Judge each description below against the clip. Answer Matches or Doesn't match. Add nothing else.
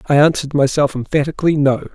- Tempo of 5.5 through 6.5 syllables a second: Doesn't match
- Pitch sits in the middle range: Matches